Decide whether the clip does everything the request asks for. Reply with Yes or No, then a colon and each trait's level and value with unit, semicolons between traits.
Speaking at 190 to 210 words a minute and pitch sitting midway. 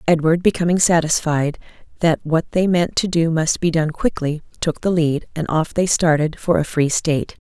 Yes: average, 195 wpm; medium, 165 Hz